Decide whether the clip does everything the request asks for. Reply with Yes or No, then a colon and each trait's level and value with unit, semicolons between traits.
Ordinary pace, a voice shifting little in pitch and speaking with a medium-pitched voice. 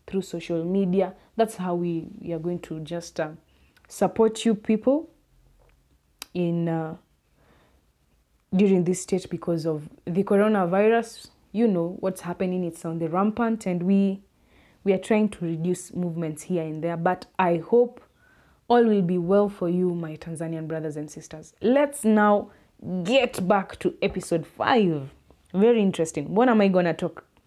No: average, 155 wpm; average, 3.7 semitones; medium, 180 Hz